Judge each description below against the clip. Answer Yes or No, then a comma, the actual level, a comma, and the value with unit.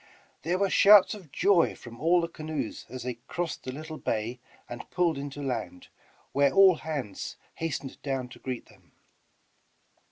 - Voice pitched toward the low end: No, medium, 145 Hz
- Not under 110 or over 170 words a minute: Yes, average, 160 wpm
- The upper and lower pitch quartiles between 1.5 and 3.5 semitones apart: No, average, 5.0 semitones